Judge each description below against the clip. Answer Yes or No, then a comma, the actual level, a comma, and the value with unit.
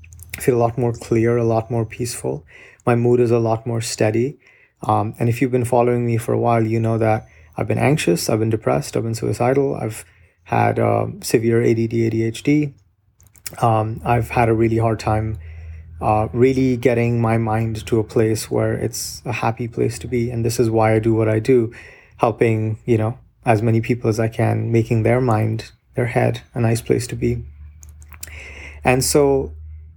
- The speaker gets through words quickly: No, average, 190 wpm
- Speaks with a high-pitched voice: No, low, 115 Hz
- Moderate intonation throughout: No, narrow, 1.6 semitones